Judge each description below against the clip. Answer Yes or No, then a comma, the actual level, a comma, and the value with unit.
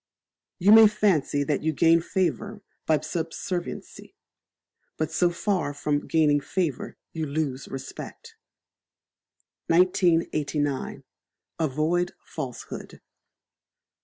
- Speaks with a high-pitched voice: No, medium, 160 Hz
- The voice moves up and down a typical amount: Yes, average, 3.4 semitones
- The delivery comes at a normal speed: No, slow, 90 wpm